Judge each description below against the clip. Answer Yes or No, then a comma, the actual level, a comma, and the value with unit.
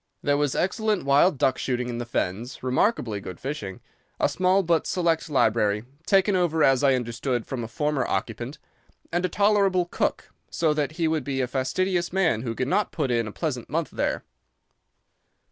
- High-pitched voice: No, medium, 145 Hz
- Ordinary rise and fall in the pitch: No, wide, 6.2 semitones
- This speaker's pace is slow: No, average, 180 wpm